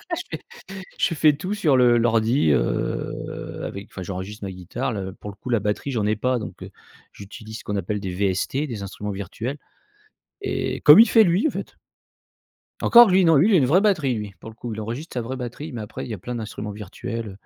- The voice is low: Yes, low, 115 Hz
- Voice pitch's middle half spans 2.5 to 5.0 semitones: No, wide, 5.5 semitones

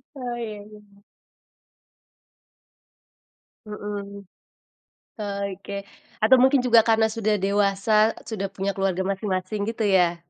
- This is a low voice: No, high, 205 Hz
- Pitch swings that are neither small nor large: No, narrow, 1.9 semitones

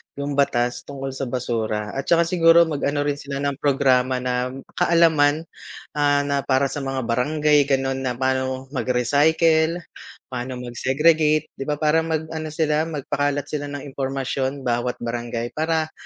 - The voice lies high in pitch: No, medium, 140 Hz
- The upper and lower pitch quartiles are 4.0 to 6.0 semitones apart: No, average, 2.8 semitones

